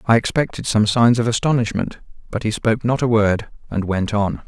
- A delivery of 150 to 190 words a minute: No, average, 200 wpm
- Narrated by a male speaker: Yes, male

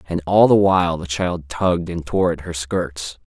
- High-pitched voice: No, very low, 85 Hz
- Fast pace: Yes, fast, 220 wpm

